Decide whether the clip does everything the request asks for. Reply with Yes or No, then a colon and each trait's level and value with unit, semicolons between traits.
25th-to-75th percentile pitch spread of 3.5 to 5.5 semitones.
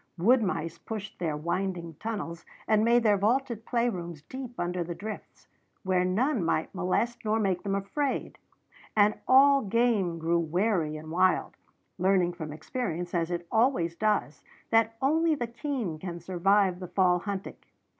Yes: average, 4.8 semitones